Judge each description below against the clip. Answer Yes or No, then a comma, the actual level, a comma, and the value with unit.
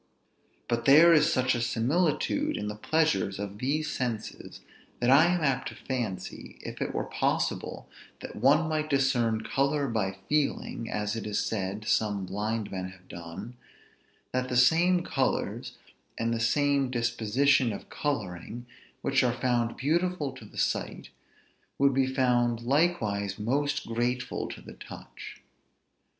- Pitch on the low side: Yes, low, 125 Hz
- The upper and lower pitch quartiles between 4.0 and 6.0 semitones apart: Yes, average, 4.5 semitones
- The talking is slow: No, average, 145 wpm